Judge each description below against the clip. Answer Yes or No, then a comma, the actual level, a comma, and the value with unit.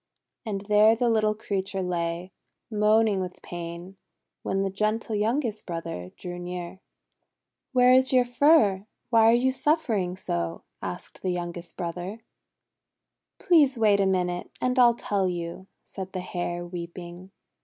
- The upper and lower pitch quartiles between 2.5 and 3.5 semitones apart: No, average, 4.2 semitones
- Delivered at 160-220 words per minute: No, average, 145 wpm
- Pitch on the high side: Yes, high, 195 Hz